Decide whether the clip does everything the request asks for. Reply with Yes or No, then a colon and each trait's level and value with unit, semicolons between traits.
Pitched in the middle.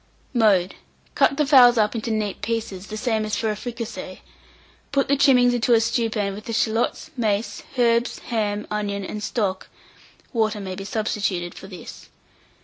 No: high, 220 Hz